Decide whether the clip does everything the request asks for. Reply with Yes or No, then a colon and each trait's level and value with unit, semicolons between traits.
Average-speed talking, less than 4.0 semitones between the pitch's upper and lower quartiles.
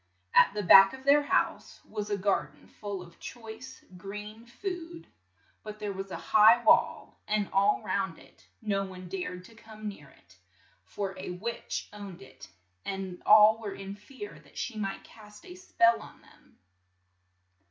Yes: average, 170 wpm; narrow, 2.6 semitones